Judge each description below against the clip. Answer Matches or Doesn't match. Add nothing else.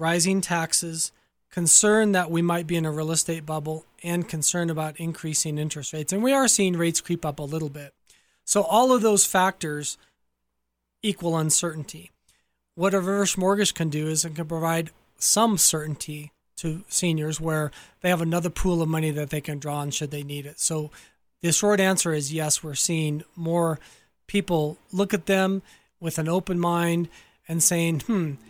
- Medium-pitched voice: Matches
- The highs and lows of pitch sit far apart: Doesn't match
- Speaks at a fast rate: Doesn't match